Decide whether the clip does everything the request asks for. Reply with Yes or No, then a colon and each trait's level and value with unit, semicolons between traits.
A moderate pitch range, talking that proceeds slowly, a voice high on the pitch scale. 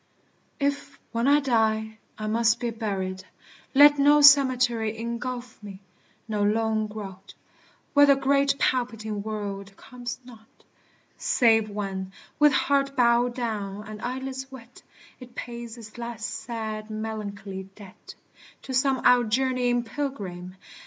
Yes: average, 3.2 semitones; slow, 125 wpm; high, 230 Hz